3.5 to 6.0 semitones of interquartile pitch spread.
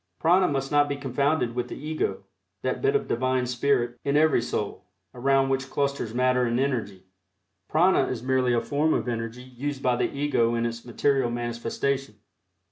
No: average, 2.9 semitones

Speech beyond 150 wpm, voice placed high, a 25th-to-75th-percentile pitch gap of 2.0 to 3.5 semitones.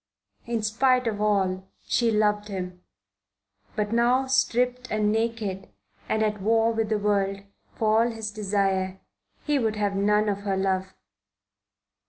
No: average, 145 wpm; high, 210 Hz; narrow, 2.5 semitones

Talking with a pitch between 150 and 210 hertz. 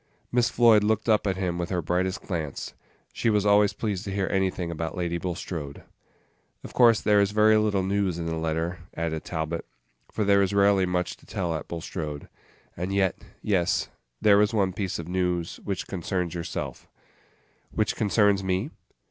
No: very low, 95 Hz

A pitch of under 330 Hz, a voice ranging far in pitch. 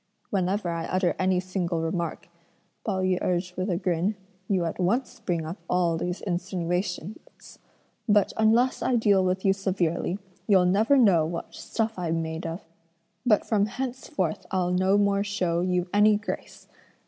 No: medium, 185 Hz; average, 2.7 semitones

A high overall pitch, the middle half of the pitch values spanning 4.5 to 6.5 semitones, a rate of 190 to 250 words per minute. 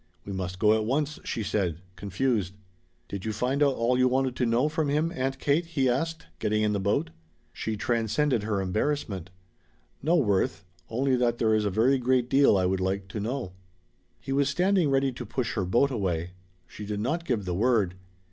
No: low, 120 Hz; average, 5.1 semitones; average, 200 wpm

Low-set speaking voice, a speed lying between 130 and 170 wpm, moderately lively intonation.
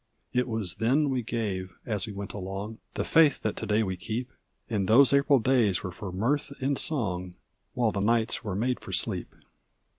No: low, 110 Hz; average, 190 wpm; average, 4.6 semitones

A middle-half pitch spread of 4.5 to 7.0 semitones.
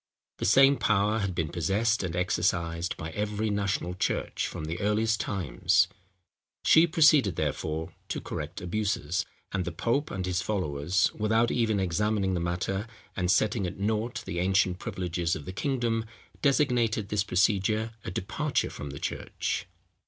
No: average, 3.8 semitones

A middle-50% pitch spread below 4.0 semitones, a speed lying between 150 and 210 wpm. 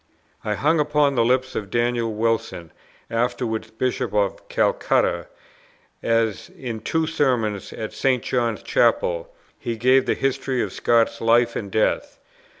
No: average, 2.9 semitones; average, 140 wpm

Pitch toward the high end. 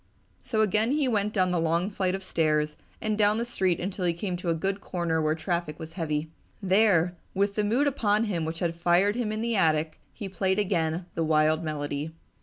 No: medium, 180 Hz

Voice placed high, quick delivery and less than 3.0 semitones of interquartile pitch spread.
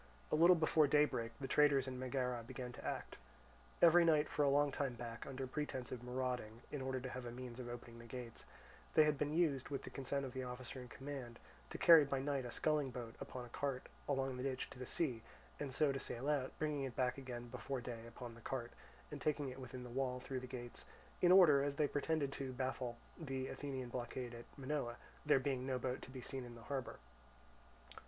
No: low, 130 Hz; fast, 225 wpm; narrow, 2.5 semitones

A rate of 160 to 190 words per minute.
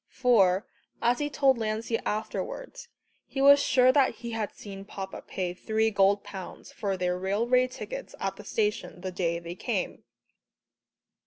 No: average, 150 wpm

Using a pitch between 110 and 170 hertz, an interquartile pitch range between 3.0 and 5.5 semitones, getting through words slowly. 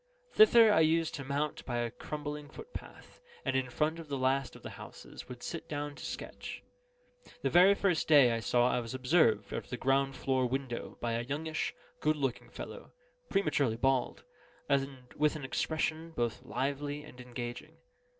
No: medium, 140 Hz; average, 3.5 semitones; average, 180 wpm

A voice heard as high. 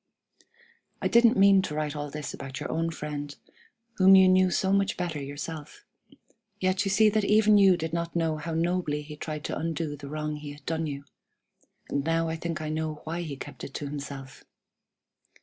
No: medium, 160 Hz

